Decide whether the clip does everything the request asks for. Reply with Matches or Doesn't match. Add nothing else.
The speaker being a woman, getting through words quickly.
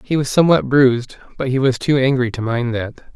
Doesn't match